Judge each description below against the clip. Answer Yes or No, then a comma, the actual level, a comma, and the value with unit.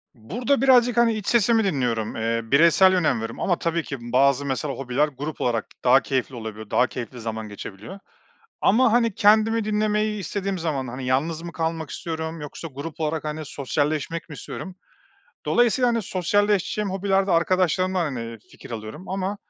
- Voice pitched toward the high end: No, medium, 160 Hz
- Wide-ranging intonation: Yes, wide, 7.4 semitones